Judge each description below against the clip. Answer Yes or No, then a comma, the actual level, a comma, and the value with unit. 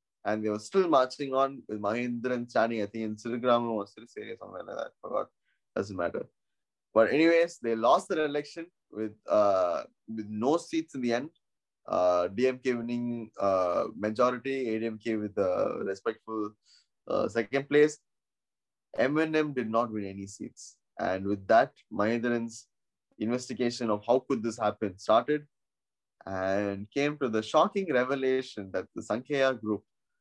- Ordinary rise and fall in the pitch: Yes, average, 4.2 semitones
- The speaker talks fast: Yes, fast, 150 wpm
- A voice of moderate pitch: No, low, 120 Hz